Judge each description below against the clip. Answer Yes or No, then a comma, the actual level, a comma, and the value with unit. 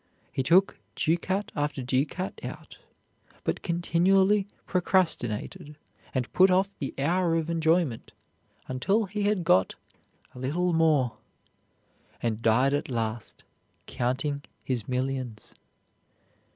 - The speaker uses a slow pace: Yes, slow, 110 wpm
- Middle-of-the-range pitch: Yes, medium, 155 Hz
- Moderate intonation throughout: No, wide, 6.0 semitones